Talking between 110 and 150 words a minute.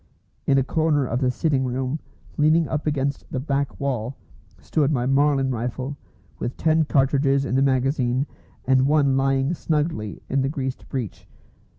No: average, 160 wpm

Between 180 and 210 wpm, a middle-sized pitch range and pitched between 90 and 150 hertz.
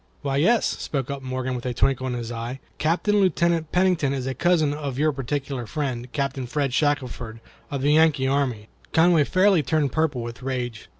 Yes: average, 185 wpm; average, 3.6 semitones; medium, 140 Hz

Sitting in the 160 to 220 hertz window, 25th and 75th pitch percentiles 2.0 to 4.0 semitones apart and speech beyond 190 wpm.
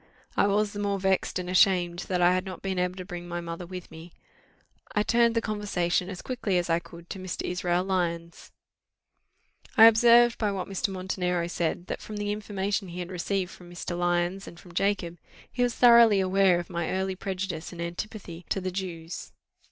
Yes: medium, 185 Hz; narrow, 2.4 semitones; average, 200 wpm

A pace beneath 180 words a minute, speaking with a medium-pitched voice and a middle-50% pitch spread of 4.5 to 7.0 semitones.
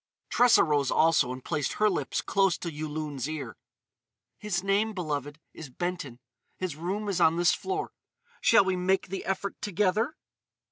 Yes: average, 155 wpm; medium, 175 Hz; average, 4.8 semitones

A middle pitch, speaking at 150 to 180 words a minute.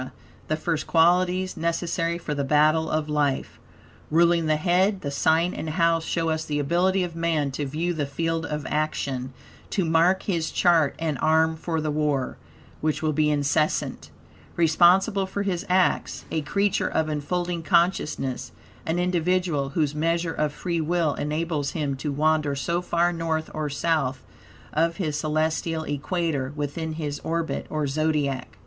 Yes: medium, 160 Hz; average, 155 wpm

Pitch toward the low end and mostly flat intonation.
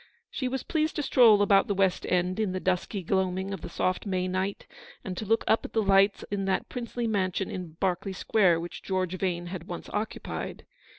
No: high, 195 Hz; narrow, 2.3 semitones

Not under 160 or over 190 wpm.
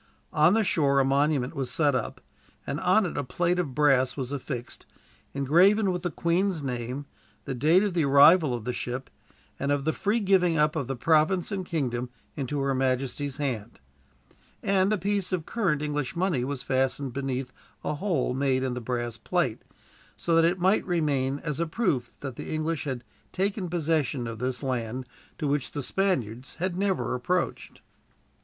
Yes: average, 180 wpm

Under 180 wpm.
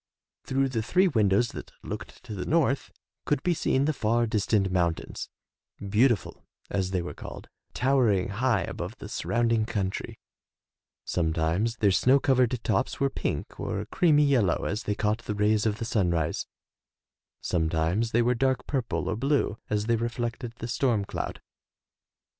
Yes: average, 155 wpm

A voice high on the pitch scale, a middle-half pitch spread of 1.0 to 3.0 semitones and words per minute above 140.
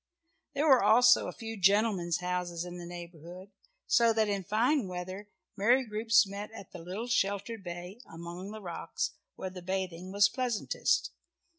No: high, 195 Hz; average, 3.8 semitones; average, 160 wpm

